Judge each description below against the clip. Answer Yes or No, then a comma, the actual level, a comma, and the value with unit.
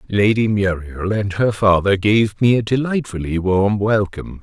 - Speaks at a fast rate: No, average, 150 wpm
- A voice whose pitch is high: No, low, 105 Hz